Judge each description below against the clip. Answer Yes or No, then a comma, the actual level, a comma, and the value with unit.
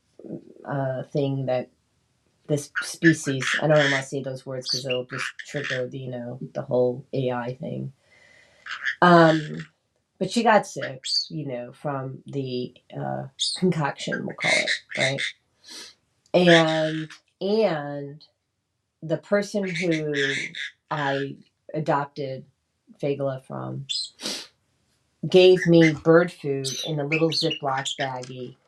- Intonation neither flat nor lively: Yes, average, 3.9 semitones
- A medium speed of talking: No, slow, 115 wpm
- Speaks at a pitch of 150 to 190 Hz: No, medium, 140 Hz